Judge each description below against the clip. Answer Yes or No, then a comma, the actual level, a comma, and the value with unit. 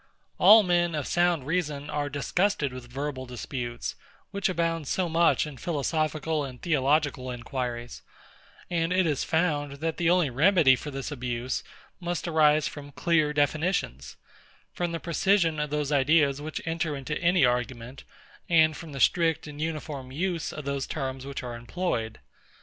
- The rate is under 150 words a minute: No, average, 155 wpm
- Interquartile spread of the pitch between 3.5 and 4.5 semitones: Yes, average, 3.8 semitones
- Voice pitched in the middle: Yes, medium, 150 Hz